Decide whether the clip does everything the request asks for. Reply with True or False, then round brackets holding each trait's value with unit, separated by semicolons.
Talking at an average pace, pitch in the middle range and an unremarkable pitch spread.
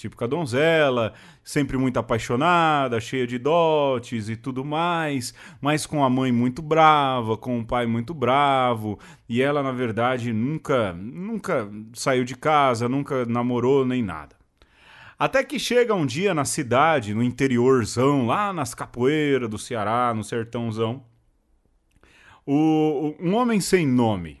False (145 wpm; 130 Hz; 3.9 semitones)